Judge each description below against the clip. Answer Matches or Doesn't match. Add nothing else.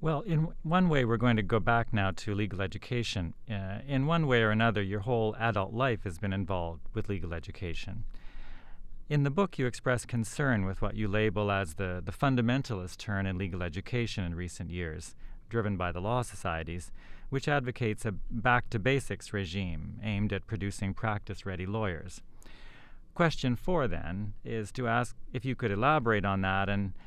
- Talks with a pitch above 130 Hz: Doesn't match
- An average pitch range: Matches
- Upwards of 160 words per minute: Matches